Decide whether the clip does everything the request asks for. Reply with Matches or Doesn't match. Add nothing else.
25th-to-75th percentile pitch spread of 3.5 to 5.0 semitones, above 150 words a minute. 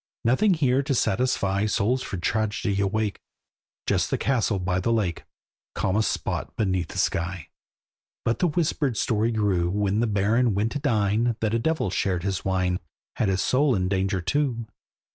Matches